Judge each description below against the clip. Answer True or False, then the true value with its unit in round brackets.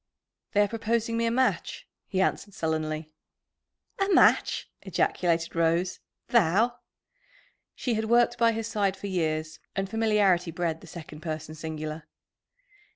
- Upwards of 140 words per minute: False (135 wpm)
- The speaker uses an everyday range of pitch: False (5.9 semitones)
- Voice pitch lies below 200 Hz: True (190 Hz)